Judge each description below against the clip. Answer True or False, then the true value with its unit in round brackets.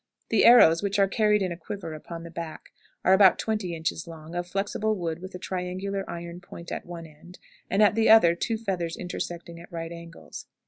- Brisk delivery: True (210 wpm)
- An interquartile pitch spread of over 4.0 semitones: False (2.9 semitones)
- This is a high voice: False (175 Hz)